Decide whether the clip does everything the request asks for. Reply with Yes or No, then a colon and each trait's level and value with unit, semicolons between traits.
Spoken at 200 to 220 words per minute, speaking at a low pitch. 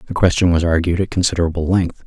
Yes: fast, 205 wpm; very low, 90 Hz